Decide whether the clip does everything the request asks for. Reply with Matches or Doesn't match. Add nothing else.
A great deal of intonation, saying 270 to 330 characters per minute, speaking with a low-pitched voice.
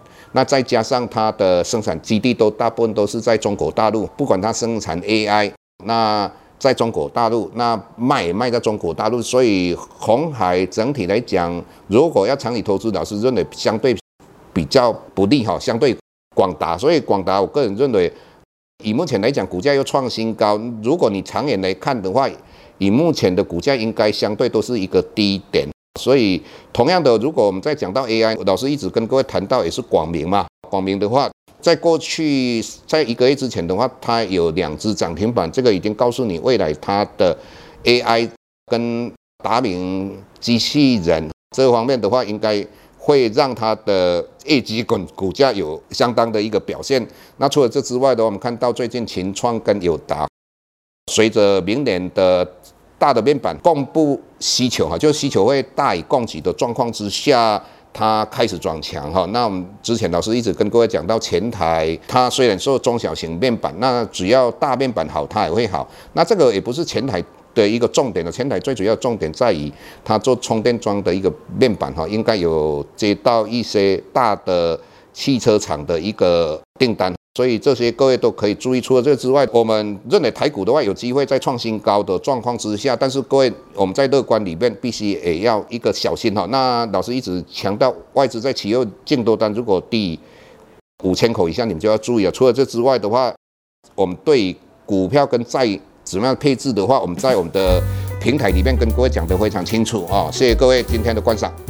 Doesn't match